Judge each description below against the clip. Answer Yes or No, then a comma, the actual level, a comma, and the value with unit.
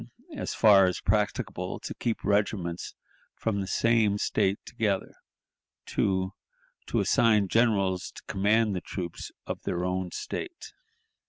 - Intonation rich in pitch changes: No, average, 2.9 semitones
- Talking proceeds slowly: Yes, slow, 130 wpm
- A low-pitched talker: Yes, low, 100 Hz